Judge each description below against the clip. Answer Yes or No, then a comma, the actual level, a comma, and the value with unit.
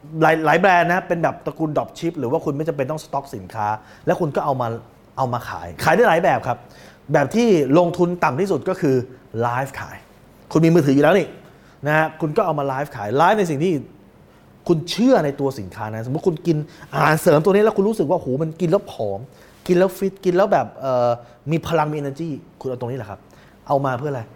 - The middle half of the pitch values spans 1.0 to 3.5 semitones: No, average, 5.1 semitones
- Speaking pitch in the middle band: Yes, medium, 155 Hz